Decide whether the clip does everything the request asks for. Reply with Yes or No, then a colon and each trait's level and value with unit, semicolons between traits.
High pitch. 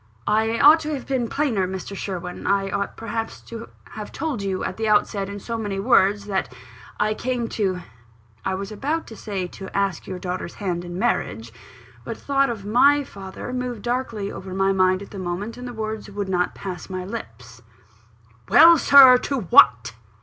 Yes: high, 200 Hz